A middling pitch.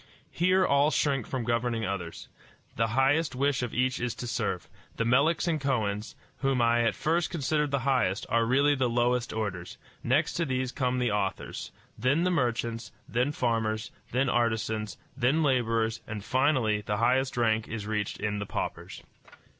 No: low, 125 Hz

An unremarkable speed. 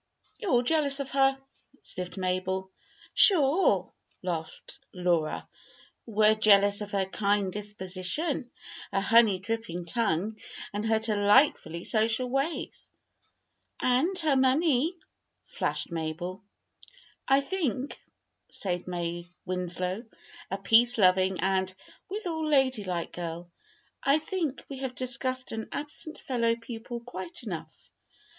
No: slow, 110 wpm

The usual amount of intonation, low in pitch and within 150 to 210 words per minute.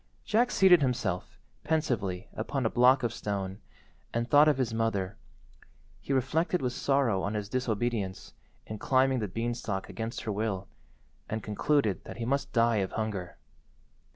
Yes: average, 4.3 semitones; low, 115 Hz; average, 155 wpm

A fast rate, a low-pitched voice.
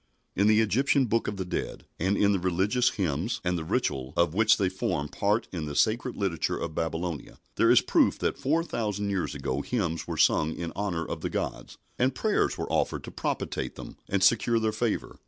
Yes: fast, 210 wpm; low, 100 Hz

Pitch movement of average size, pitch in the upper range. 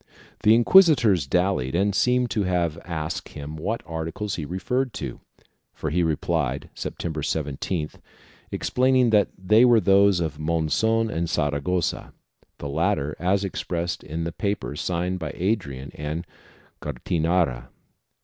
No: average, 4.7 semitones; very low, 85 Hz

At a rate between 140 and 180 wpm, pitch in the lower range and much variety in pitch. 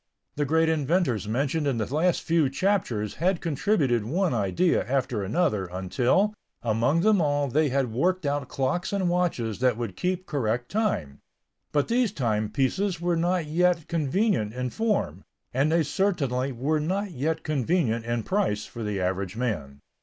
No: average, 160 wpm; medium, 145 Hz; wide, 7.1 semitones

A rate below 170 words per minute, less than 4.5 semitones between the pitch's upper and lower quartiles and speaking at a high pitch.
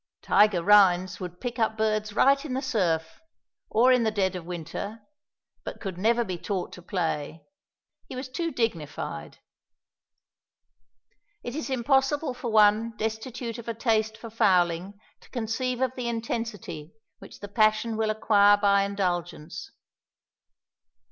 Yes: average, 140 wpm; average, 4.0 semitones; high, 215 Hz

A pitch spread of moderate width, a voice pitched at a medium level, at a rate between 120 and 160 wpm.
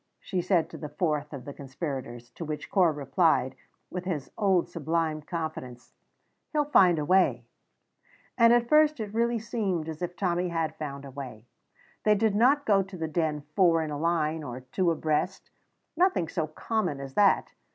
No: average, 4.7 semitones; medium, 165 Hz; average, 180 wpm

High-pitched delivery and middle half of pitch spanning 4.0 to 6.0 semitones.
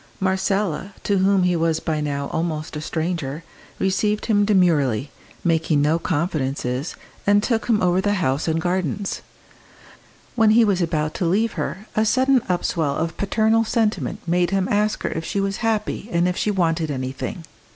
No: medium, 180 Hz; average, 4.3 semitones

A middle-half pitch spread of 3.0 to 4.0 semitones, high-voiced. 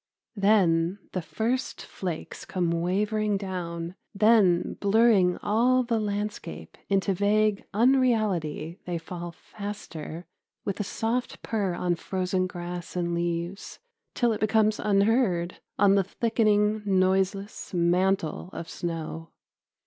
Yes: average, 3.5 semitones; high, 195 Hz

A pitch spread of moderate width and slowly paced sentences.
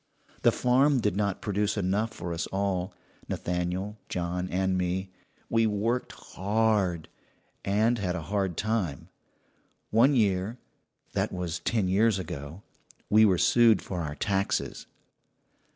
Yes: average, 3.3 semitones; slow, 130 wpm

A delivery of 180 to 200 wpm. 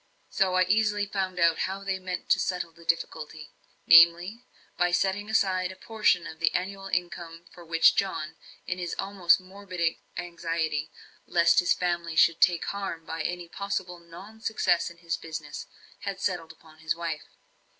No: average, 160 wpm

